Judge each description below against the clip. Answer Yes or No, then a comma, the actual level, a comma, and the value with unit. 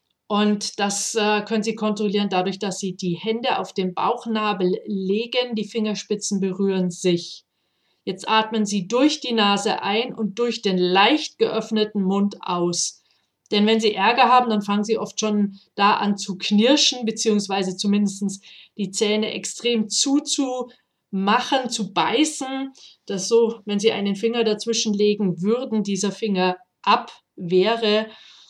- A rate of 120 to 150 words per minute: Yes, average, 140 wpm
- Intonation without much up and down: Yes, narrow, 2.3 semitones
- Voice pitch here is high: Yes, high, 210 Hz